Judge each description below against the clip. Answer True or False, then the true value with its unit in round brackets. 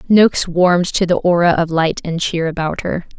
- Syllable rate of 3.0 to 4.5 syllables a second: False (5.2 syllables/s)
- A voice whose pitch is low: False (170 Hz)